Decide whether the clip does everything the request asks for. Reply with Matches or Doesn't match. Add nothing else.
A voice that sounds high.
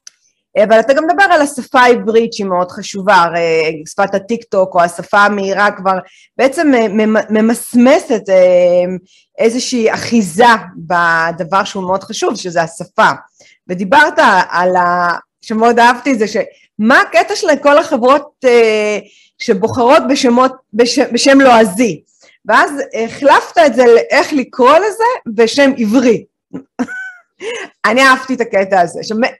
Matches